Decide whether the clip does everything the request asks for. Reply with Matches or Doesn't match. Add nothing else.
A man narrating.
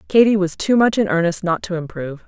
Doesn't match